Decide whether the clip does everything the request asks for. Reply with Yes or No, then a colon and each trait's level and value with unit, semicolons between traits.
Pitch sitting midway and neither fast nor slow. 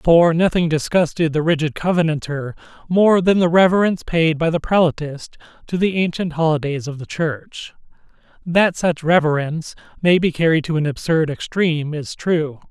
Yes: medium, 160 Hz; average, 155 wpm